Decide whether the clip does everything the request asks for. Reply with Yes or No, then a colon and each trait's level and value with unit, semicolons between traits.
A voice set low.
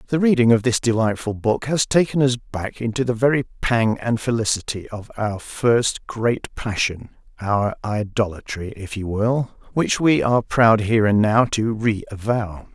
Yes: low, 115 Hz